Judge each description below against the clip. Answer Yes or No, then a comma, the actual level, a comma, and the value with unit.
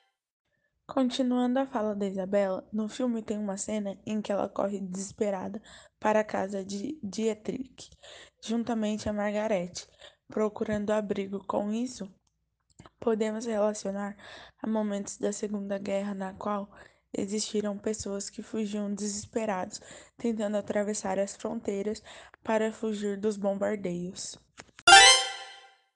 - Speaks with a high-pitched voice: Yes, high, 210 Hz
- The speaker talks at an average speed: No, slow, 115 wpm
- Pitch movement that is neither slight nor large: No, narrow, 1.7 semitones